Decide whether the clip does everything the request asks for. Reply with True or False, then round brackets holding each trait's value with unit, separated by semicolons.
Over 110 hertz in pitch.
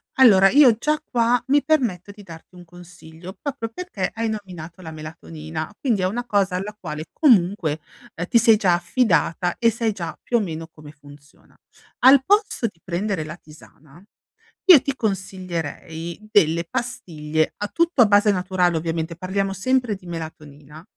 True (185 Hz)